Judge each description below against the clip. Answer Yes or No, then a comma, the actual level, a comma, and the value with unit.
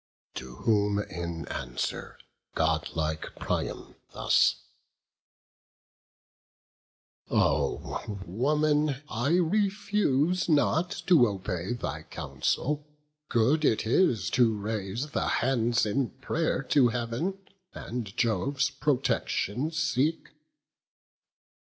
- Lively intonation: Yes, wide, 6.6 semitones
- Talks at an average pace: No, slow, 85 wpm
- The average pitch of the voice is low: Yes, low, 125 Hz